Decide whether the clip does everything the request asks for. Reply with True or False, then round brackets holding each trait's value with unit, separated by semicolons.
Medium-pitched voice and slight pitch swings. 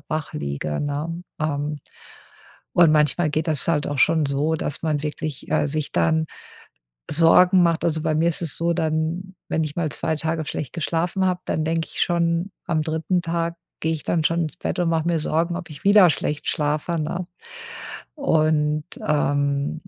True (160 Hz; 2.0 semitones)